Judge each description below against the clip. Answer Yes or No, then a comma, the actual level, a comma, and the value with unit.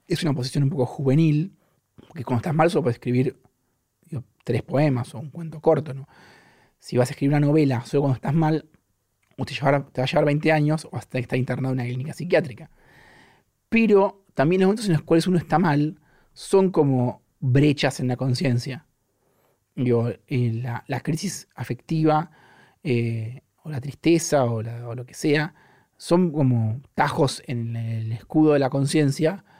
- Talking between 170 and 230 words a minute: Yes, average, 175 wpm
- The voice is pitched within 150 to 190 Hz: No, medium, 140 Hz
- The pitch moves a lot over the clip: No, average, 3.9 semitones